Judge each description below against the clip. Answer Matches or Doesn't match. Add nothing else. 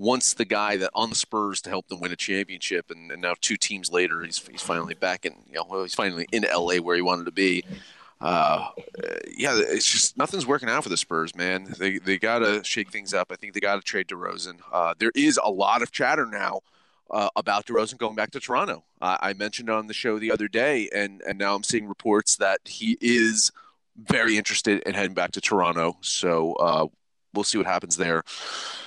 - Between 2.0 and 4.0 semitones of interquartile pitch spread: Matches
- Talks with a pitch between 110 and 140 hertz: Doesn't match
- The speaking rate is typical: Doesn't match